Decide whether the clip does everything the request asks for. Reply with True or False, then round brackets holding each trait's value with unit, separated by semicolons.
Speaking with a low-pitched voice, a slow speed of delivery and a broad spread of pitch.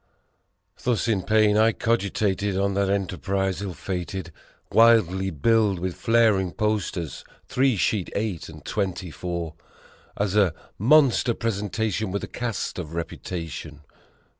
False (100 Hz; 130 wpm; 3.4 semitones)